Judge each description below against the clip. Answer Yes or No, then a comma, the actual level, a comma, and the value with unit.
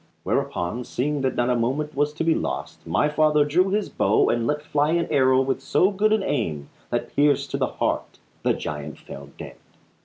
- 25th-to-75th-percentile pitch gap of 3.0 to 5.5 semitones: Yes, average, 4.1 semitones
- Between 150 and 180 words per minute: No, fast, 205 wpm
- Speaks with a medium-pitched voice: Yes, medium, 145 Hz